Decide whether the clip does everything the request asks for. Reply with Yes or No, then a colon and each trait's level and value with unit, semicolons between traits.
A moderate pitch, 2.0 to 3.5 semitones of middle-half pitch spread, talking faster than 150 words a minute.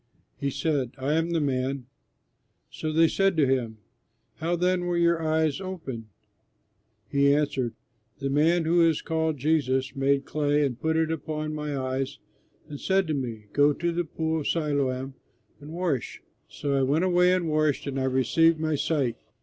Yes: medium, 150 Hz; average, 3.2 semitones; average, 175 wpm